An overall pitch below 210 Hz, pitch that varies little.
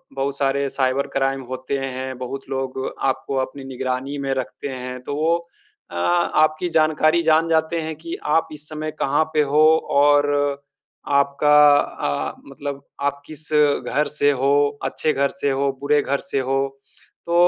Yes: medium, 140 Hz; narrow, 2.0 semitones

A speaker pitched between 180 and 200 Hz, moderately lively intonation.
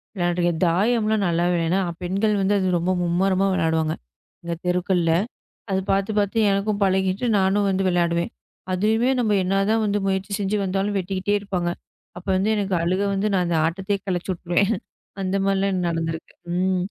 No: high, 190 Hz; narrow, 2.3 semitones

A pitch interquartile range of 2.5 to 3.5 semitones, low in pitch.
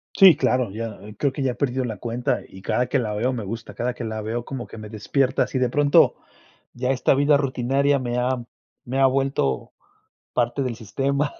Yes: average, 2.9 semitones; low, 125 Hz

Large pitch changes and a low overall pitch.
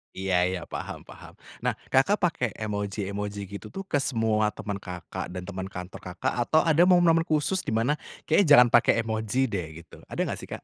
Yes: wide, 7.3 semitones; low, 110 Hz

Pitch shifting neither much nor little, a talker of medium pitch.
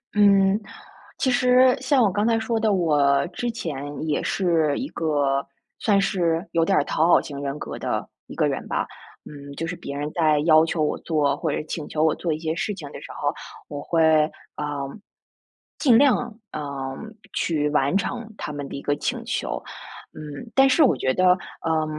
No: wide, 6.1 semitones; medium, 160 Hz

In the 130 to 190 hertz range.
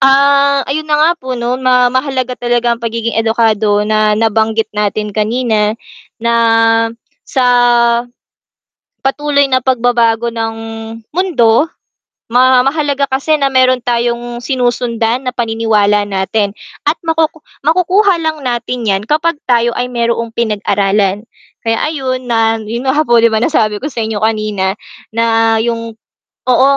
No: high, 240 Hz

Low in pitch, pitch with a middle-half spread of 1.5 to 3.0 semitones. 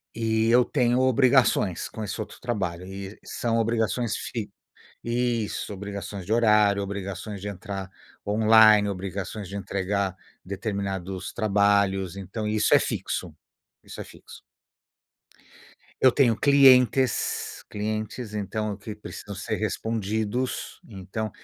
Yes: low, 105 Hz; narrow, 2.5 semitones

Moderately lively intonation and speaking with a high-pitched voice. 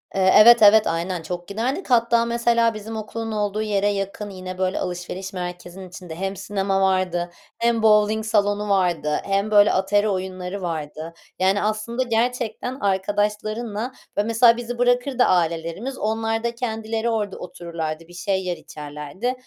Yes: average, 3.5 semitones; high, 205 Hz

